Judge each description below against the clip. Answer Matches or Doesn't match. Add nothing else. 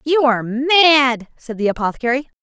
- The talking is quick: Doesn't match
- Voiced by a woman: Matches